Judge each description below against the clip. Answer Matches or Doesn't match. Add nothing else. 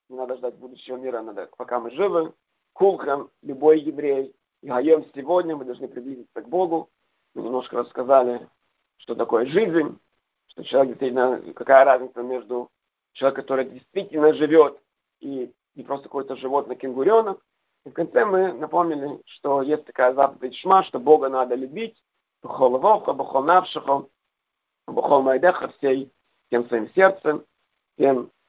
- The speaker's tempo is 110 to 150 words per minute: Matches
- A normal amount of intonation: Matches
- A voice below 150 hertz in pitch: Matches